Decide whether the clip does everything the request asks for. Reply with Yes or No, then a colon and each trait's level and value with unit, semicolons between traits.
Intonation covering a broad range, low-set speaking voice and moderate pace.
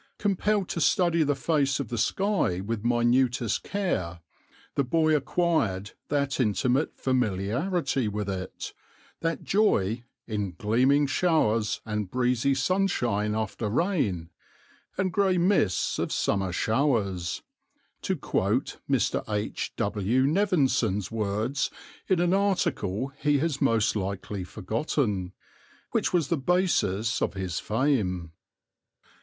No: wide, 7.4 semitones; low, 125 Hz; slow, 115 wpm